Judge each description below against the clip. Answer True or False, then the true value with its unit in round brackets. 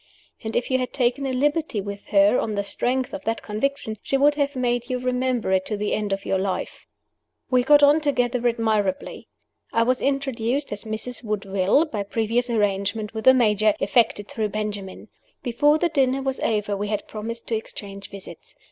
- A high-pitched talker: True (230 Hz)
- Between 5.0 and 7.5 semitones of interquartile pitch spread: False (3.9 semitones)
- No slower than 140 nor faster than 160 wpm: False (190 wpm)